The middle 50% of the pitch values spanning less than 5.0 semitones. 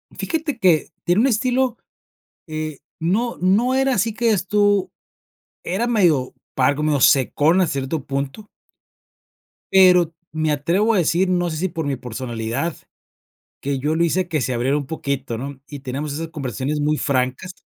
No: wide, 5.4 semitones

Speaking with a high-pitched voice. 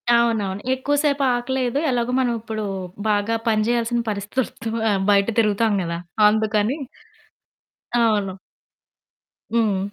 Yes: high, 225 Hz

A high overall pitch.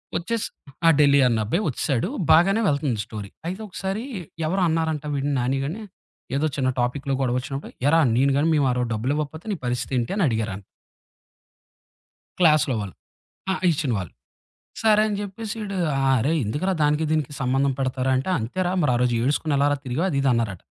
No: medium, 140 Hz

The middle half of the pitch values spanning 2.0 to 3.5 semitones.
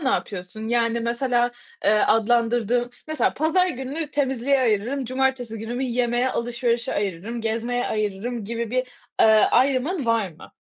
Yes: narrow, 2.5 semitones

